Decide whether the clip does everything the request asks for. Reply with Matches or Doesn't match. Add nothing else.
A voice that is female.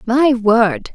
Matches